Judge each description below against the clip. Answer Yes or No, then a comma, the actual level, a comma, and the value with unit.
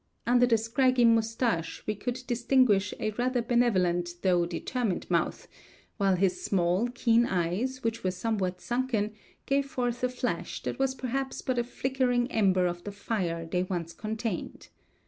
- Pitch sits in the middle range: No, high, 225 Hz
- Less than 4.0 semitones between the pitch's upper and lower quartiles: No, average, 5.0 semitones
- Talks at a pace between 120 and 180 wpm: Yes, average, 155 wpm